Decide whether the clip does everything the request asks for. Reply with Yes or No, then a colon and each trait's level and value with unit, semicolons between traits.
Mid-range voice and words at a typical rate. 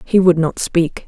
No: medium, 170 Hz; fast, 225 wpm